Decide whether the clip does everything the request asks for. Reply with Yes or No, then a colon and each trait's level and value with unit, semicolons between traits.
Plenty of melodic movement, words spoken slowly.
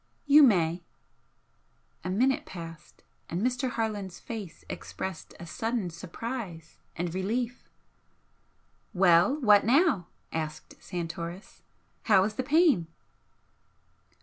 Yes: wide, 6.2 semitones; slow, 100 wpm